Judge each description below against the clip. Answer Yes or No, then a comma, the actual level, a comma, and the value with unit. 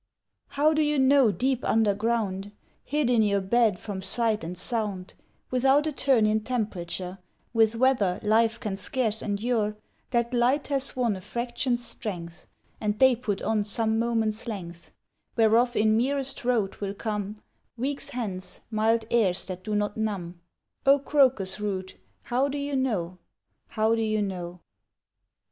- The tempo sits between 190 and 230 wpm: No, average, 150 wpm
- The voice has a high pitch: Yes, high, 220 Hz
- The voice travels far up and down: No, average, 3.7 semitones